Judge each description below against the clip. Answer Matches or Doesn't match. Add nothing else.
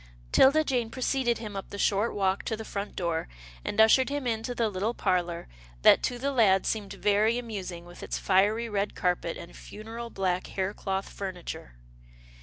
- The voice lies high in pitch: Matches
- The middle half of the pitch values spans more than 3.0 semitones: Matches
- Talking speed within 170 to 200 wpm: Matches